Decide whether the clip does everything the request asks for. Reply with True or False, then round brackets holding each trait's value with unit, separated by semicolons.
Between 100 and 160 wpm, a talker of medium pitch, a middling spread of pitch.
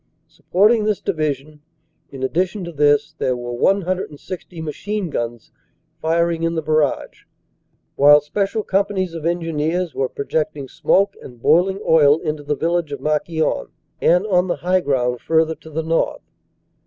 True (145 wpm; 160 Hz; 3.5 semitones)